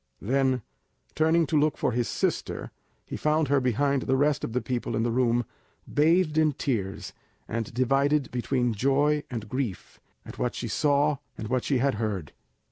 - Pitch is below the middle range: Yes, low, 130 Hz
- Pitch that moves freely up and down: No, average, 3.7 semitones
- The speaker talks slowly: No, average, 175 wpm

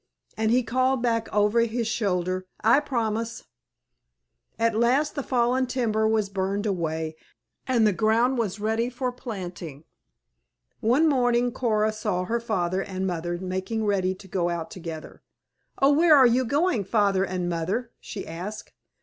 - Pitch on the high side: Yes, high, 220 Hz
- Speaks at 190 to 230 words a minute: No, average, 150 wpm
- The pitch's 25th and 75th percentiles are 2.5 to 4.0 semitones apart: No, average, 4.4 semitones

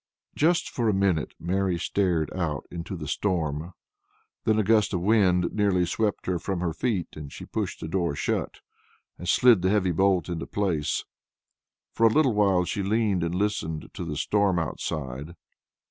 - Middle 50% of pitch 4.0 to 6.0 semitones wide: No, average, 3.6 semitones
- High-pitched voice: No, very low, 90 Hz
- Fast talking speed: No, average, 175 wpm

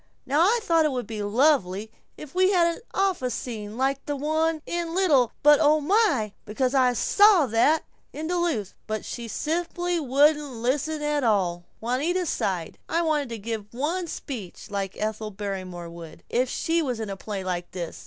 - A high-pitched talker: Yes, very high, 265 Hz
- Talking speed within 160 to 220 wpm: Yes, average, 180 wpm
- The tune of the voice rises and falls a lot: Yes, wide, 7.1 semitones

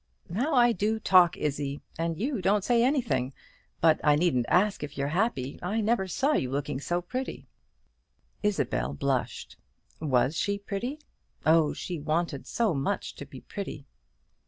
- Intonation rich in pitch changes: Yes, wide, 6.8 semitones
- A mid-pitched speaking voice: Yes, medium, 170 Hz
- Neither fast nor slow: Yes, average, 155 wpm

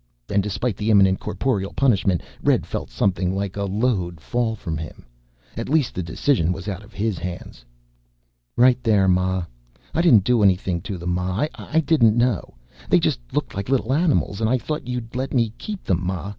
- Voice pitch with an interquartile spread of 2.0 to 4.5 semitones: No, average, 5.0 semitones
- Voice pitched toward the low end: Yes, low, 100 Hz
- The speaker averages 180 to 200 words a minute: Yes, average, 190 wpm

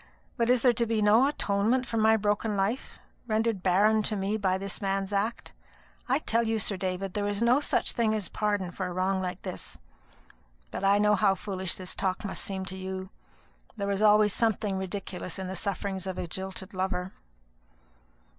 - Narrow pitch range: Yes, narrow, 2.3 semitones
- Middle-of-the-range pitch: No, high, 200 Hz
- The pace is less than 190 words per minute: No, average, 195 wpm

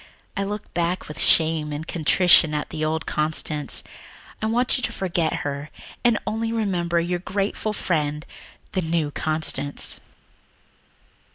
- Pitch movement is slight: No, average, 4.3 semitones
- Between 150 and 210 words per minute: No, slow, 135 wpm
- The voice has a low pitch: No, medium, 170 Hz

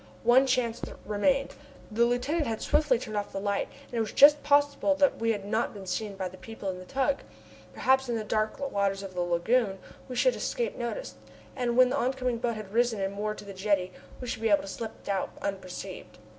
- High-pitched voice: Yes, high, 225 Hz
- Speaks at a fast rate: Yes, fast, 220 wpm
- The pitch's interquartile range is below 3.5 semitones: No, average, 4.3 semitones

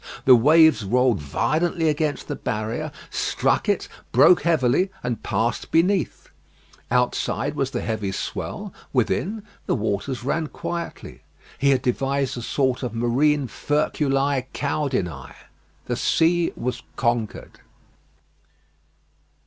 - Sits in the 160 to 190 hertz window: No, low, 135 Hz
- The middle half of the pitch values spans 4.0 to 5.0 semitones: Yes, average, 4.5 semitones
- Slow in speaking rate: Yes, slow, 115 wpm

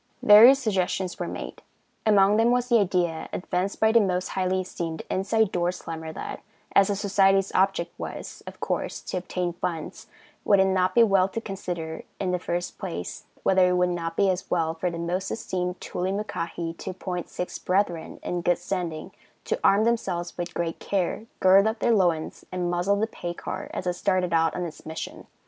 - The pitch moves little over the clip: Yes, narrow, 2.2 semitones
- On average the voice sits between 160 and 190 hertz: Yes, medium, 185 Hz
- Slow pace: No, average, 190 wpm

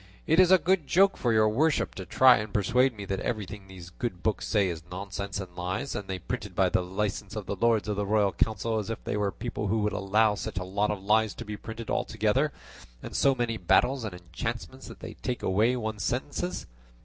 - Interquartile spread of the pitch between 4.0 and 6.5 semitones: No, average, 3.5 semitones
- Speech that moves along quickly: Yes, fast, 230 wpm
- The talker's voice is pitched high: No, low, 105 Hz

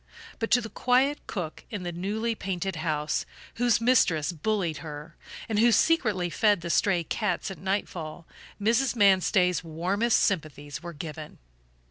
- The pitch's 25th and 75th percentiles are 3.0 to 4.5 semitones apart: No, average, 5.0 semitones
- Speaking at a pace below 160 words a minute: Yes, average, 145 wpm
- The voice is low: No, high, 190 Hz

